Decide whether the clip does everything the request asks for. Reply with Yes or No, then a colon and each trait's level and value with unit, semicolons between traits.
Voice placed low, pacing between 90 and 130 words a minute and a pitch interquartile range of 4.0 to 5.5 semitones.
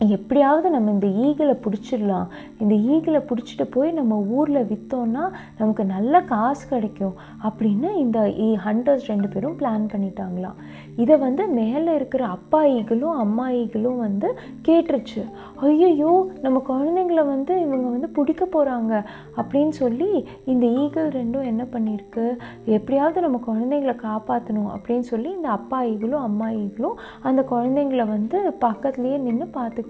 No: high, 245 Hz; average, 120 wpm; average, 4.8 semitones